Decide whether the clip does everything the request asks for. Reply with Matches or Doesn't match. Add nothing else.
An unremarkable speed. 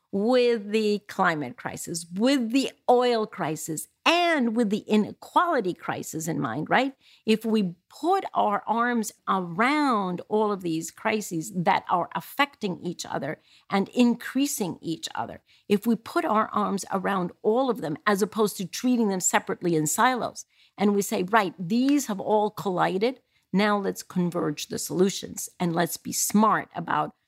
Matches